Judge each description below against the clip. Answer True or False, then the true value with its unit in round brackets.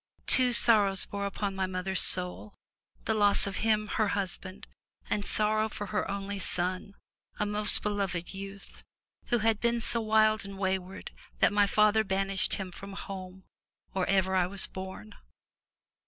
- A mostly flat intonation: True (2.0 semitones)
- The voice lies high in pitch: True (200 Hz)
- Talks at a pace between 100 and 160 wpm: True (155 wpm)